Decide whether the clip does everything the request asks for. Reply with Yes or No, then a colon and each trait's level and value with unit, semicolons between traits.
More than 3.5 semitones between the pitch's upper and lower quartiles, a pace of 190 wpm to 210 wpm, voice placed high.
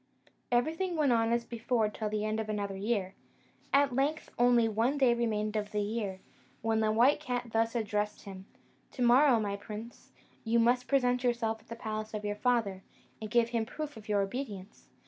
No: narrow, 2.6 semitones; average, 195 wpm; high, 225 Hz